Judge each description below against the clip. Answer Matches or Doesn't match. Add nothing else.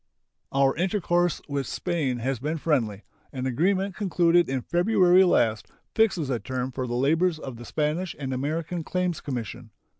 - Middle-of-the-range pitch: Matches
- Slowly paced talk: Doesn't match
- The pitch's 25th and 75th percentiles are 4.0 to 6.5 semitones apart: Matches